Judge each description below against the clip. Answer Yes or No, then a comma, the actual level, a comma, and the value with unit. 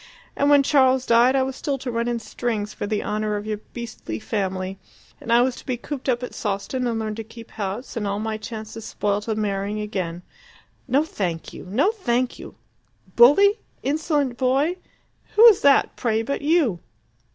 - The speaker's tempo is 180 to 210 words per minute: Yes, average, 185 wpm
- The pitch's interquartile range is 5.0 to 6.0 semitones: No, average, 4.1 semitones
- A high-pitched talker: Yes, high, 235 Hz